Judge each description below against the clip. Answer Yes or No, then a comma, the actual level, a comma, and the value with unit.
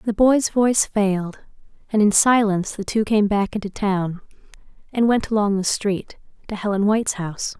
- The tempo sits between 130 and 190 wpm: Yes, average, 175 wpm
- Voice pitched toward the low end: No, high, 205 Hz